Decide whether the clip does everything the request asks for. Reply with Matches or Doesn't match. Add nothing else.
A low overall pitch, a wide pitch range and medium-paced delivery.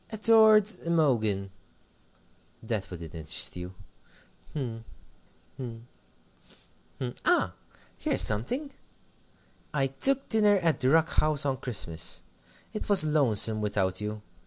Doesn't match